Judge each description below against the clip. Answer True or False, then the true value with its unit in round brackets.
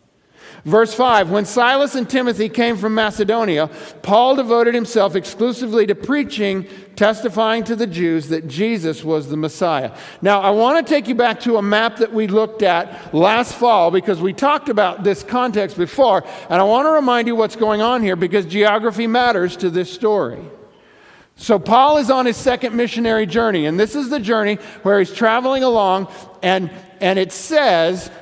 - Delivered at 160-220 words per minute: True (180 wpm)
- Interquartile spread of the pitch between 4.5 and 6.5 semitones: False (4.1 semitones)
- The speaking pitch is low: False (215 Hz)